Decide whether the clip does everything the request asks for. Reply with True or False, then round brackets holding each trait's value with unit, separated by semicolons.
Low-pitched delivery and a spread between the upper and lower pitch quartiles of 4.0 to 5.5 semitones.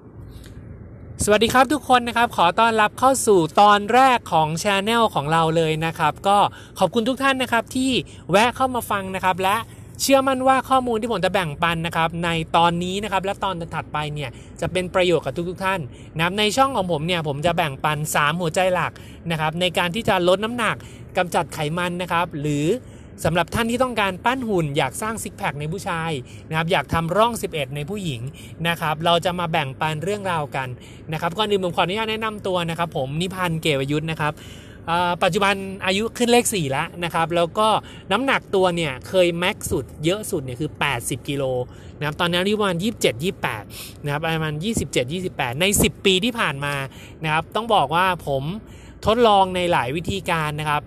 False (175 Hz; 5.0 semitones)